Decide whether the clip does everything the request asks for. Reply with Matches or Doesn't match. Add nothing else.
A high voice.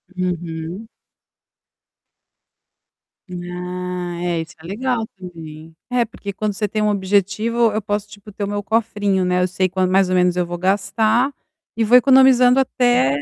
Matches